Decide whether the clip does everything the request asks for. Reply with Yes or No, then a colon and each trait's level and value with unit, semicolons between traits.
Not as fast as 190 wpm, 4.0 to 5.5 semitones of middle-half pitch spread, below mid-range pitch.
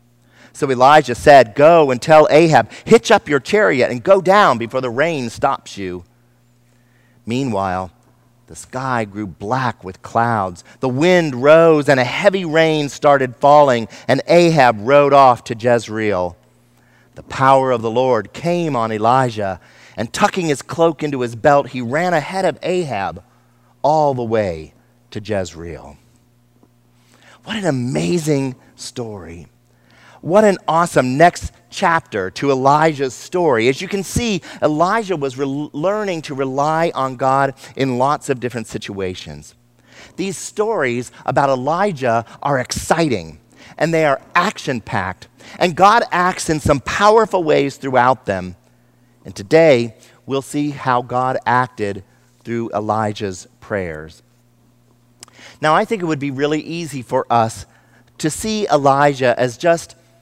Yes: average, 140 wpm; average, 4.7 semitones; low, 130 Hz